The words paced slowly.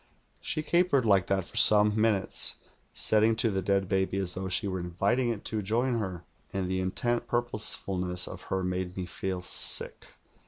No: average, 180 wpm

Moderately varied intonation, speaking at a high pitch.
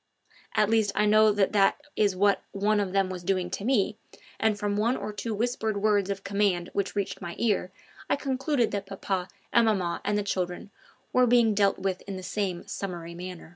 No: narrow, 2.2 semitones; high, 200 Hz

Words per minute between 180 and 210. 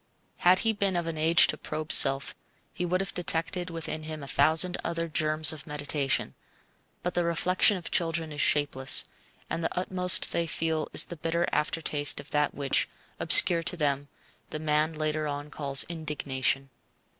No: average, 170 wpm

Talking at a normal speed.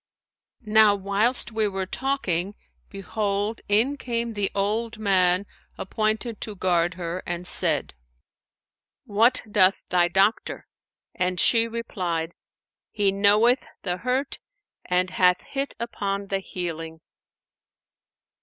No: slow, 110 wpm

